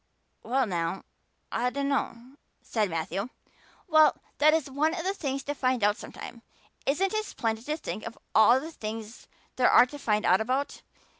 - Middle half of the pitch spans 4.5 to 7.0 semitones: Yes, average, 4.9 semitones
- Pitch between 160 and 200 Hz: No, very high, 255 Hz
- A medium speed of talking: Yes, average, 170 wpm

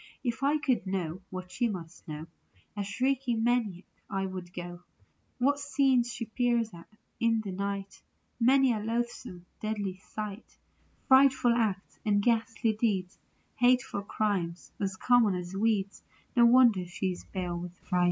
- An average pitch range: Yes, average, 4.4 semitones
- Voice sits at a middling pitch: No, high, 210 Hz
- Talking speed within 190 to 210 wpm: No, average, 150 wpm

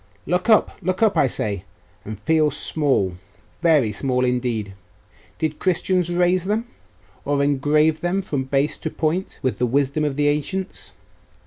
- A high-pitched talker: No, medium, 150 Hz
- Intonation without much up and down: No, average, 5.1 semitones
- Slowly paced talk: No, average, 150 wpm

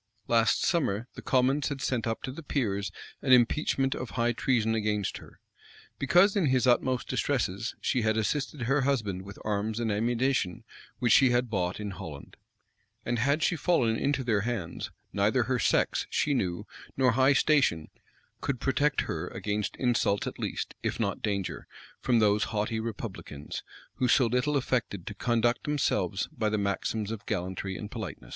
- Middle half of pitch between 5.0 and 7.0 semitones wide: No, average, 4.2 semitones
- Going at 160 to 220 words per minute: Yes, average, 170 wpm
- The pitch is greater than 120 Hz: No, low, 115 Hz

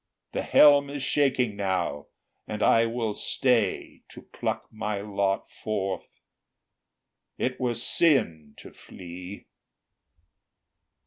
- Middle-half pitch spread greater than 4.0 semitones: Yes, average, 4.6 semitones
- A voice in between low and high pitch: No, low, 105 Hz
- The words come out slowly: Yes, slow, 105 wpm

